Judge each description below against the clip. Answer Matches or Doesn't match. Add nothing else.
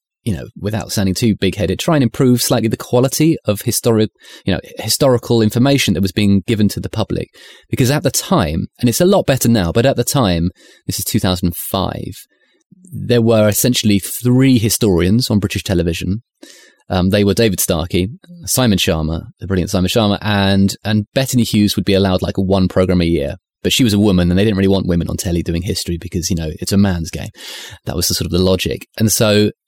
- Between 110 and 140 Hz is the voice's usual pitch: Doesn't match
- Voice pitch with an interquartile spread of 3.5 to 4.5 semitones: Matches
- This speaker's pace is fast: Matches